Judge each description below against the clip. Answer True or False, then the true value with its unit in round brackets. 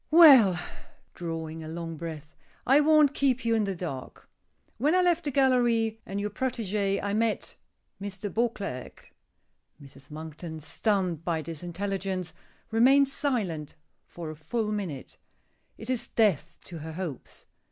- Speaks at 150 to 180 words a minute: False (140 wpm)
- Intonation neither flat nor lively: False (6.5 semitones)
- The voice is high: True (195 Hz)